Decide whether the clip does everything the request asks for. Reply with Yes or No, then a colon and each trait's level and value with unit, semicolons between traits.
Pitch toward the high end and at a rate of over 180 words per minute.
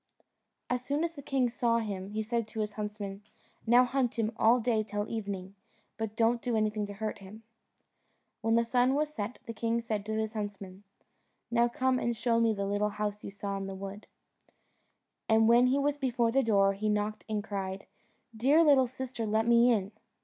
Yes: high, 220 Hz; average, 200 wpm